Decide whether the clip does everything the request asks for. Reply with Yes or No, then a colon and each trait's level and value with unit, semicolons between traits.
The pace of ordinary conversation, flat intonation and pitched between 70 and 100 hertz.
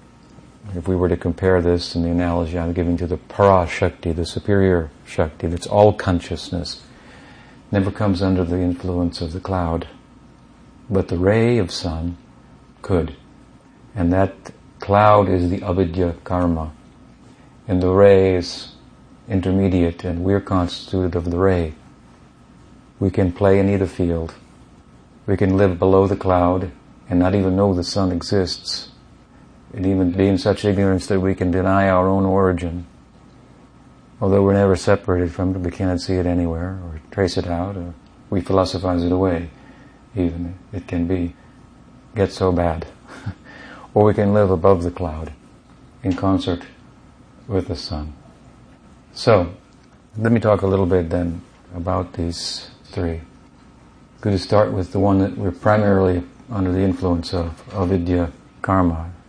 Yes: average, 155 wpm; narrow, 2.0 semitones; very low, 90 Hz